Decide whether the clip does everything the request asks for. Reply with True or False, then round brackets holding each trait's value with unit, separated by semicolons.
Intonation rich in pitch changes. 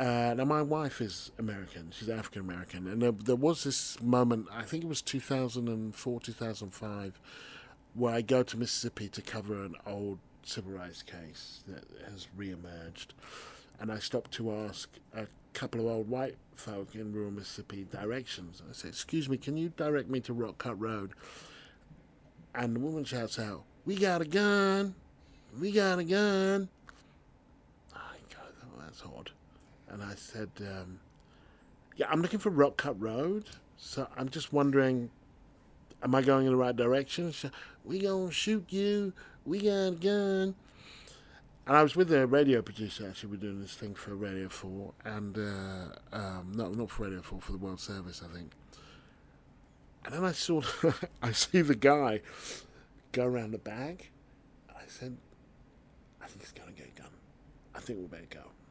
True (6.0 semitones)